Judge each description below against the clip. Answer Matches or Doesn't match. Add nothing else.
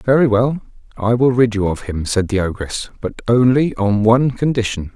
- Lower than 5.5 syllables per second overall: Matches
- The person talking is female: Doesn't match